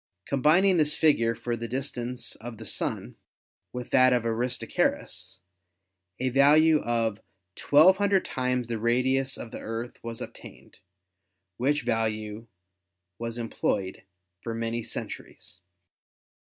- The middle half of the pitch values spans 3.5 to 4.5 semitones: No, average, 2.9 semitones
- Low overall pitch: Yes, low, 120 Hz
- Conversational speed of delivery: No, slow, 120 wpm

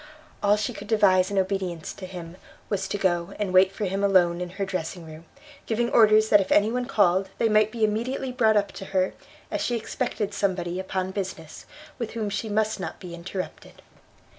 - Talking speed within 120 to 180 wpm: No, average, 200 wpm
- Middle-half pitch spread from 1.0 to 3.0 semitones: Yes, average, 2.7 semitones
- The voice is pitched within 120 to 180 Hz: No, high, 195 Hz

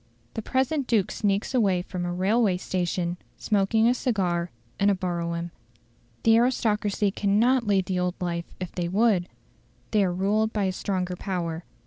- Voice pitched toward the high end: Yes, high, 195 Hz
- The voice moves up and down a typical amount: Yes, average, 3.4 semitones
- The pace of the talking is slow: No, average, 160 wpm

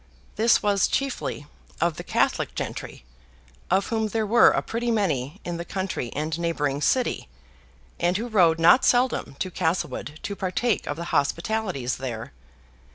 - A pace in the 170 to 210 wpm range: No, average, 155 wpm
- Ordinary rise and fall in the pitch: No, wide, 6.3 semitones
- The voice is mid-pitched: Yes, medium, 180 Hz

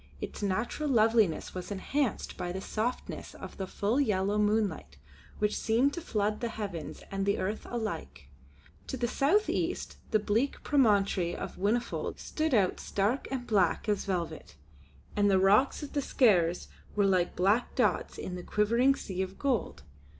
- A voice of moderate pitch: No, high, 210 Hz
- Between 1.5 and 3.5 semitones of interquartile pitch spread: No, average, 4.1 semitones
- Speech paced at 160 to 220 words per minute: Yes, average, 165 wpm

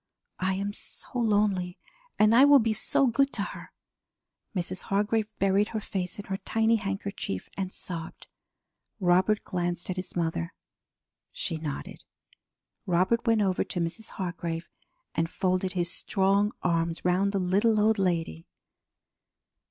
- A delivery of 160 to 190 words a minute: No, average, 140 wpm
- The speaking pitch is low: No, high, 190 Hz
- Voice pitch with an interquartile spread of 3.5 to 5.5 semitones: No, average, 3.1 semitones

